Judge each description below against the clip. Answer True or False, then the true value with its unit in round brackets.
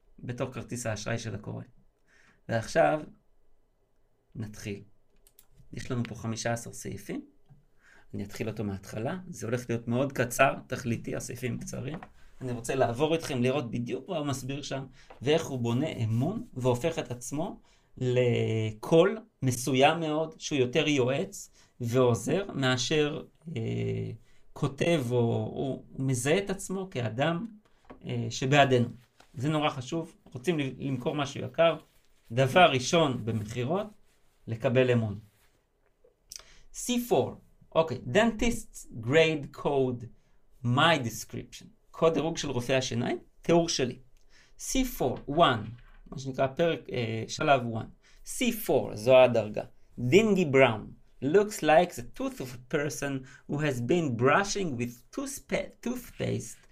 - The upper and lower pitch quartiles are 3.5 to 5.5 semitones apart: True (4.8 semitones)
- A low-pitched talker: True (130 Hz)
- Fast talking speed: False (120 wpm)